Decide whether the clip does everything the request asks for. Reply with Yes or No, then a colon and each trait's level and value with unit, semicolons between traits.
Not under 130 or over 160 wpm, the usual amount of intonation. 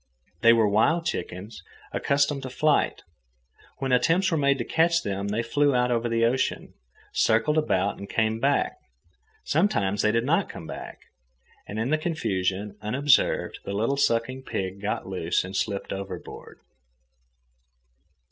No: average, 145 wpm; wide, 5.7 semitones